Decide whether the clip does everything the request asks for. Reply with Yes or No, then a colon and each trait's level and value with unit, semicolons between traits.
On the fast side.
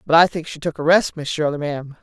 Yes: fast, 295 wpm